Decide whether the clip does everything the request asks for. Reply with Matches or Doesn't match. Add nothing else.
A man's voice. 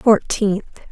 Doesn't match